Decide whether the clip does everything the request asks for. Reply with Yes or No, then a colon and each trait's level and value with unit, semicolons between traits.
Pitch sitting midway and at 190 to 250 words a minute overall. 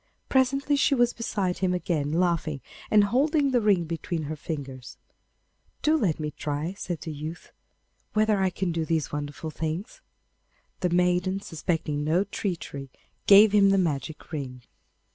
No: medium, 175 Hz; average, 150 wpm